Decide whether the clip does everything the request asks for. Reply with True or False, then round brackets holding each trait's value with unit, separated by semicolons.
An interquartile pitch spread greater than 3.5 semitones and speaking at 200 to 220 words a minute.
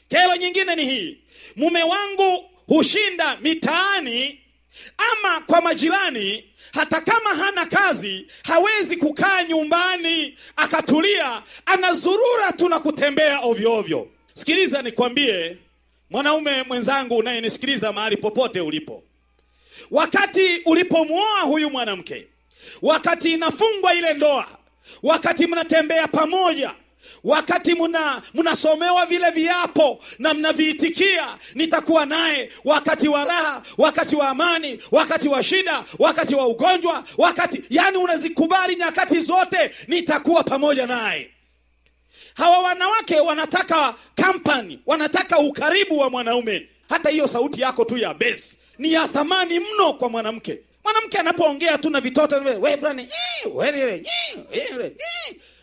False (4.0 semitones; 105 wpm)